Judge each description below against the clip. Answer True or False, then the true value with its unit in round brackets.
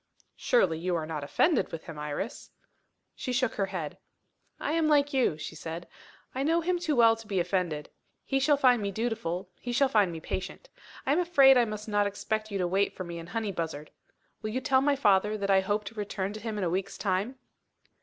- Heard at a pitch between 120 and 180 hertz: False (210 Hz)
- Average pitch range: False (6.1 semitones)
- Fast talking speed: True (220 wpm)